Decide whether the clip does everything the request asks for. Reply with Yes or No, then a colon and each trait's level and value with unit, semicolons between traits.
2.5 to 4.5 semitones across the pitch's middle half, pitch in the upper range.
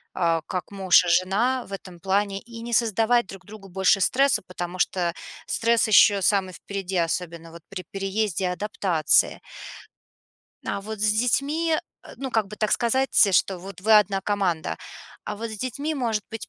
Yes: average, 3.6 semitones; high, 200 Hz